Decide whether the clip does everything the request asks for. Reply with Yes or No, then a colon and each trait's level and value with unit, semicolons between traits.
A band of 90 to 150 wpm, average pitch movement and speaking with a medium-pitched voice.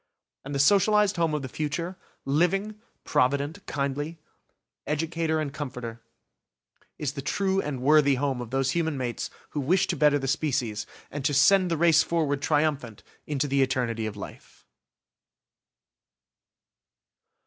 Yes: average, 140 wpm; average, 3.6 semitones; medium, 145 Hz